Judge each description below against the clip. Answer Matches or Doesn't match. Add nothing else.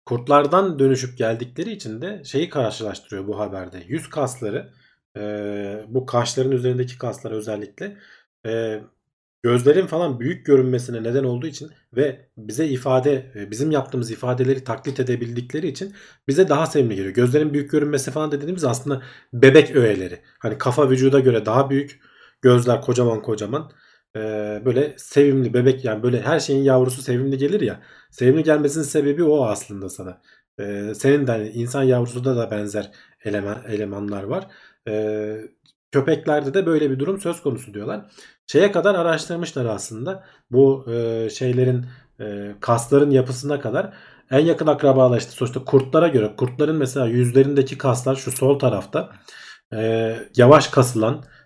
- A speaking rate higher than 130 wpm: Matches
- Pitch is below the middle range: Matches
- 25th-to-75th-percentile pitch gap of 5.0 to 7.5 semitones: Doesn't match